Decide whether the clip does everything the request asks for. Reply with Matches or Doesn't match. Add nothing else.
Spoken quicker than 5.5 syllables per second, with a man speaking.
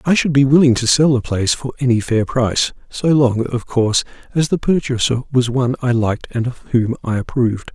Matches